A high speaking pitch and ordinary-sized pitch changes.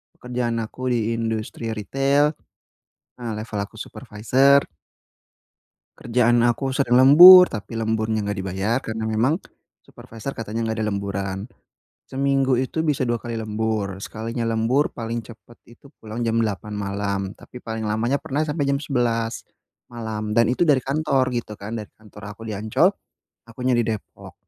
No: low, 115 Hz; average, 3.0 semitones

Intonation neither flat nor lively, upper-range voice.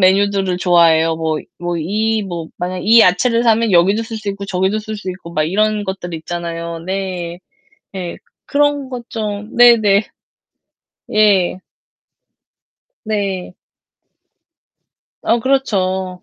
Yes: average, 3.6 semitones; high, 195 Hz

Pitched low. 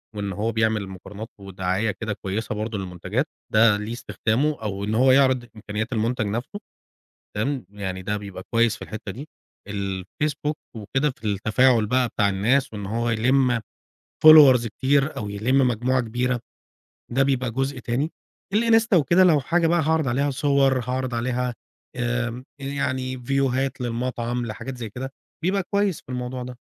Yes: low, 120 Hz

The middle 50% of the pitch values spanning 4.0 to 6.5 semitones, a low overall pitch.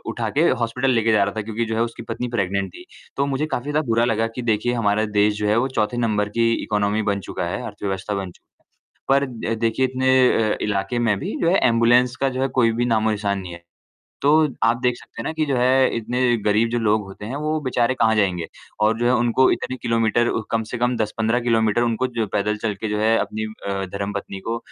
No: average, 2.7 semitones; low, 115 Hz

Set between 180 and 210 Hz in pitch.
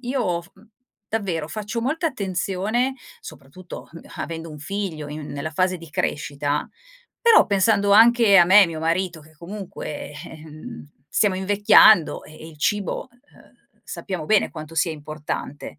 Yes: medium, 185 Hz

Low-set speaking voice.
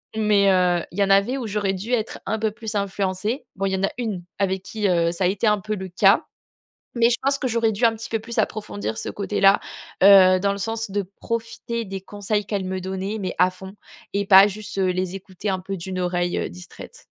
No: high, 200 Hz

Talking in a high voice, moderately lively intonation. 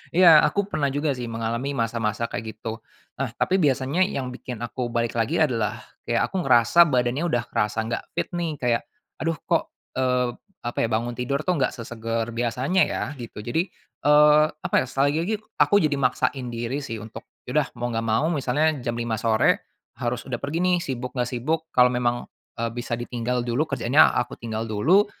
No: low, 125 Hz; average, 3.6 semitones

